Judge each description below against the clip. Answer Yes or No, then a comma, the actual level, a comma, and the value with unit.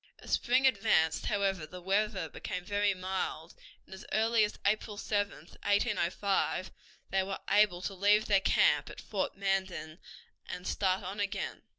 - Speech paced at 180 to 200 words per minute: No, average, 155 wpm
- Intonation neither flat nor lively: No, narrow, 2.0 semitones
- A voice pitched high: Yes, high, 195 Hz